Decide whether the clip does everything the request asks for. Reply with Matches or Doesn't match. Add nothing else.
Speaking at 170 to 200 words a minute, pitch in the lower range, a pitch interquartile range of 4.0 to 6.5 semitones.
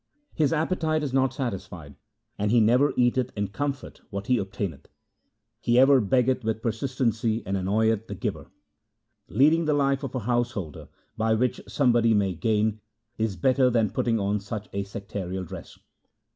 Doesn't match